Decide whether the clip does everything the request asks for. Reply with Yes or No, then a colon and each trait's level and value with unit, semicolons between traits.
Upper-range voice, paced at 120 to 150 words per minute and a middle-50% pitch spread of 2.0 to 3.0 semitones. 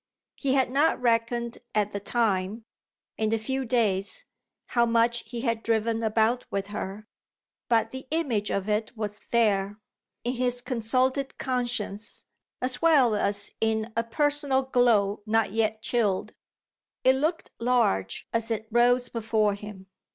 Yes: high, 230 Hz; average, 145 wpm; average, 2.7 semitones